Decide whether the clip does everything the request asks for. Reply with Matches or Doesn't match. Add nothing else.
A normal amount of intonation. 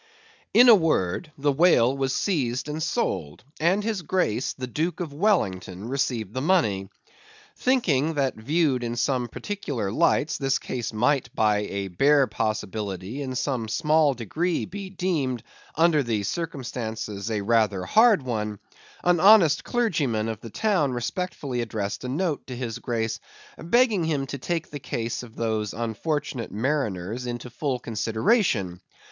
Doesn't match